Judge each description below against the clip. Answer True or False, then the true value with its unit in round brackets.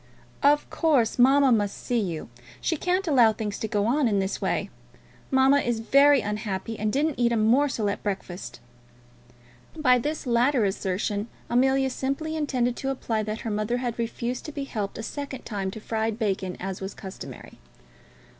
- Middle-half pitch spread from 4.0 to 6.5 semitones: True (4.5 semitones)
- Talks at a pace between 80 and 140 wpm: False (175 wpm)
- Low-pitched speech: False (235 Hz)